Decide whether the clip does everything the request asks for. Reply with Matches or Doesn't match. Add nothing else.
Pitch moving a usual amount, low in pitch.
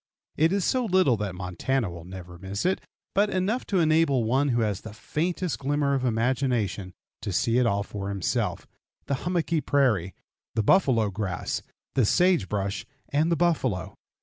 Doesn't match